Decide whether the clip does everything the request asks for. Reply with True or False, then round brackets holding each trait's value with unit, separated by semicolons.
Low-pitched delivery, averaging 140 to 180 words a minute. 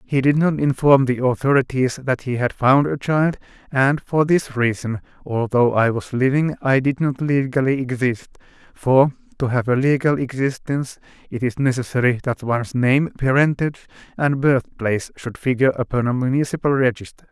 True (130 Hz; 160 wpm)